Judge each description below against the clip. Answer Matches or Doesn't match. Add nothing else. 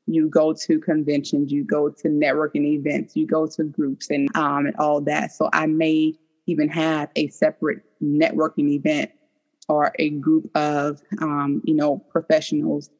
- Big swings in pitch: Matches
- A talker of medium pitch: Matches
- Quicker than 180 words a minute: Doesn't match